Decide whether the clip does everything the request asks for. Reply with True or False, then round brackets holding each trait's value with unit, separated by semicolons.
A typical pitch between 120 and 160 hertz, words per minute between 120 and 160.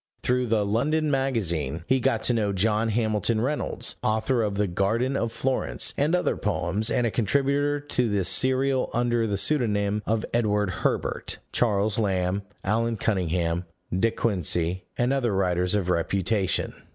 False (110 Hz; 150 wpm)